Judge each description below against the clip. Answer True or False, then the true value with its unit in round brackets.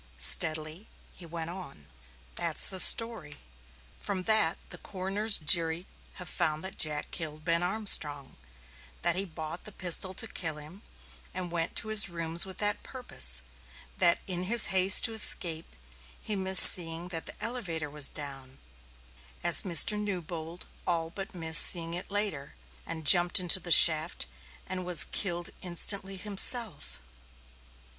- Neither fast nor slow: True (145 wpm)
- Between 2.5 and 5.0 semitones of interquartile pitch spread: True (3.2 semitones)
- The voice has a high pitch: False (175 Hz)